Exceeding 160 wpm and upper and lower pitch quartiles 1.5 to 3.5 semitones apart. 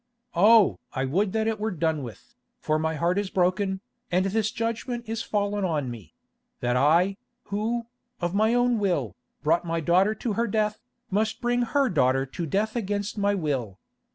No: average, 175 wpm; average, 5.3 semitones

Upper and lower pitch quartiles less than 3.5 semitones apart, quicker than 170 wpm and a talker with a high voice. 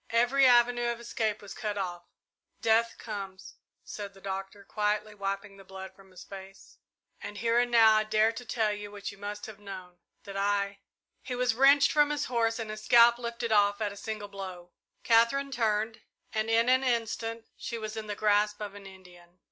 Yes: average, 2.8 semitones; average, 200 wpm; high, 215 Hz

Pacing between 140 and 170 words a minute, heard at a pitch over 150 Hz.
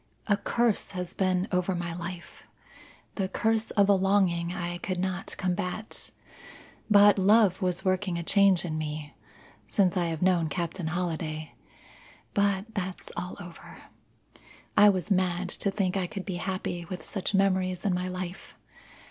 Yes: average, 155 wpm; medium, 185 Hz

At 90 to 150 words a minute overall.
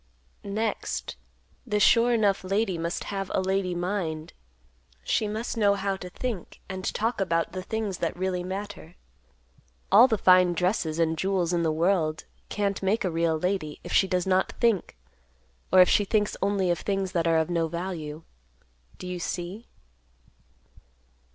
No: average, 165 wpm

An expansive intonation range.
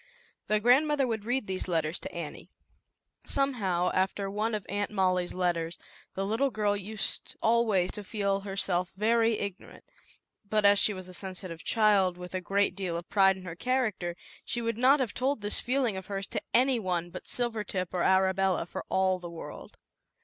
No: average, 3.4 semitones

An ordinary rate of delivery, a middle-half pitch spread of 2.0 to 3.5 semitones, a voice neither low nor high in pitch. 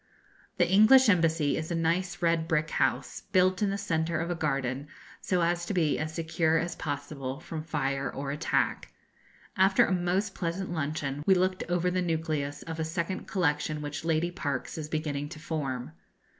Yes: average, 180 wpm; average, 3.1 semitones; medium, 165 Hz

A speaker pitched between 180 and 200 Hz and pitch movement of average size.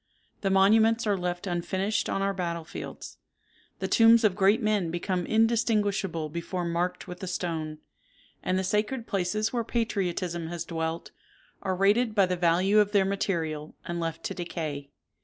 Yes: medium, 185 Hz; average, 3.5 semitones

